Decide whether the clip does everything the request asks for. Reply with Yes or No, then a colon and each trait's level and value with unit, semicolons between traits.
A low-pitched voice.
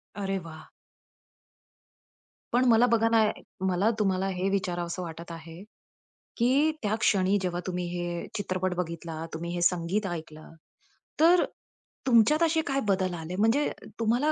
No: medium, 185 Hz